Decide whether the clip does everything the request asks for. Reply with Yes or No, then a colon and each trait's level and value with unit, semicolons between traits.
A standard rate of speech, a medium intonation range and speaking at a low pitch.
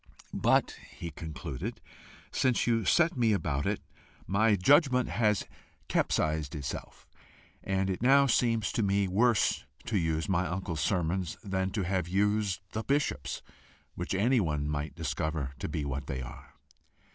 No: average, 145 wpm; wide, 6.1 semitones; very low, 95 Hz